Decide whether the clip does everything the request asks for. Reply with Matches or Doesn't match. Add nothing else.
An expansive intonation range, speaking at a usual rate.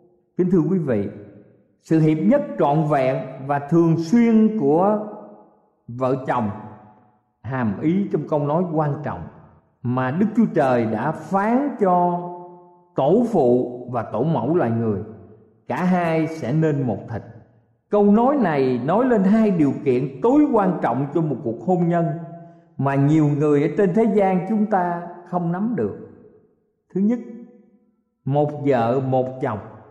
Doesn't match